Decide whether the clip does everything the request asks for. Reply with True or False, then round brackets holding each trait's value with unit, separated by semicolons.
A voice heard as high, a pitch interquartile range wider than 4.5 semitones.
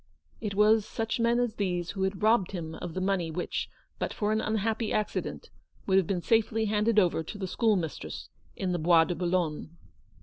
False (195 Hz; 3.6 semitones)